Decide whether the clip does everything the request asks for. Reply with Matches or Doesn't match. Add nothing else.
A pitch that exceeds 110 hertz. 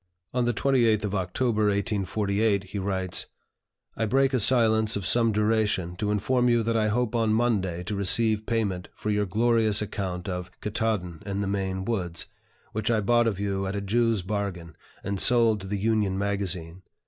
Doesn't match